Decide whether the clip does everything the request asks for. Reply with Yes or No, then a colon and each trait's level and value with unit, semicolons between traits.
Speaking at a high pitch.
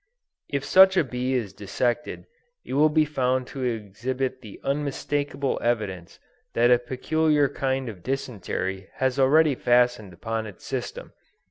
No: low, 130 Hz